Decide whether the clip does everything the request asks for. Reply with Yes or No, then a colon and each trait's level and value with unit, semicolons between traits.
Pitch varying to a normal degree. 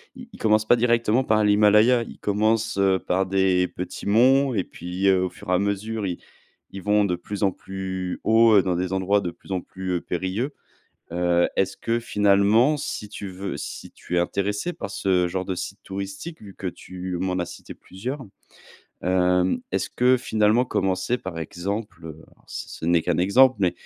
Yes: average, 3.0 semitones